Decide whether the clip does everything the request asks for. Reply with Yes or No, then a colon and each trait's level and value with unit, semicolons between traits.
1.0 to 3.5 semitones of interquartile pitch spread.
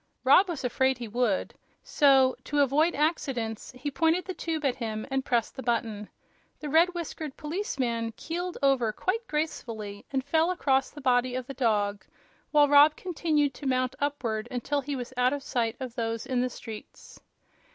No: average, 3.9 semitones